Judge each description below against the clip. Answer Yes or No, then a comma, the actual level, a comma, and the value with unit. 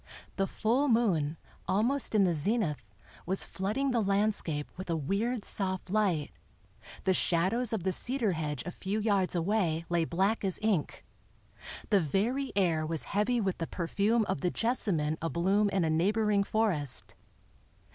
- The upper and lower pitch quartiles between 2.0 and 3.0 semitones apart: No, average, 4.4 semitones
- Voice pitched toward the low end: No, high, 195 Hz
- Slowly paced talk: No, average, 155 wpm